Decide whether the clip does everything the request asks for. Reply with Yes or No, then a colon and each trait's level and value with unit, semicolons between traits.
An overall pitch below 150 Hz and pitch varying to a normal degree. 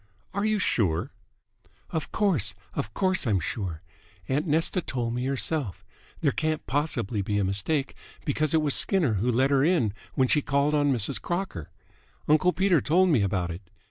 No: medium, 140 Hz; wide, 7.3 semitones